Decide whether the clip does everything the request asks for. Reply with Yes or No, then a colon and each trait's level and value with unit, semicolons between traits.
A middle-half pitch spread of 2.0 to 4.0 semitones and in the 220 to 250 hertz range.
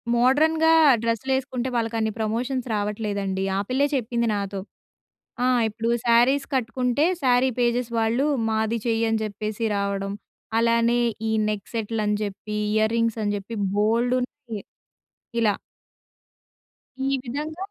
Yes: average, 2.8 semitones; high, 230 Hz